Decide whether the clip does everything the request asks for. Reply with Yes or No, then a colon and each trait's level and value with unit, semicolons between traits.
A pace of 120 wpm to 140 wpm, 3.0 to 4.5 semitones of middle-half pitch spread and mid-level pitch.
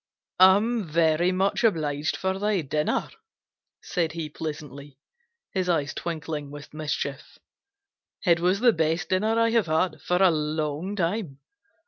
Yes: slow, 135 wpm; average, 3.8 semitones; medium, 165 Hz